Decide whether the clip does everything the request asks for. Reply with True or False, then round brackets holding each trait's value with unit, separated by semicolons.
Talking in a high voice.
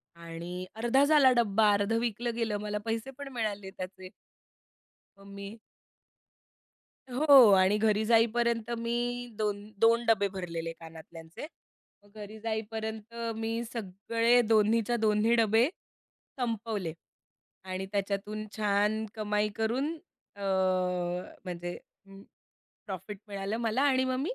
True (215 Hz)